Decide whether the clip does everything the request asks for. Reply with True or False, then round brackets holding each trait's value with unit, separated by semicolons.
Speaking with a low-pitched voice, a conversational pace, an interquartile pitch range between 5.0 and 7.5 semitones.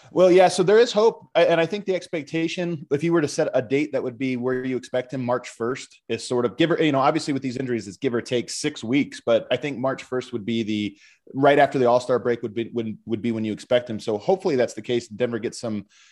False (130 Hz; 270 wpm; 5.4 semitones)